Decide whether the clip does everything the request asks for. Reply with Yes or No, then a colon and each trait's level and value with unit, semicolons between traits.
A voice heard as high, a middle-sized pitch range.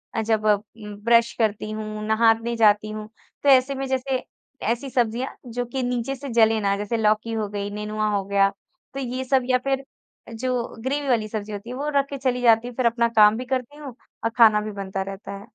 Yes: high, 230 Hz; average, 3.0 semitones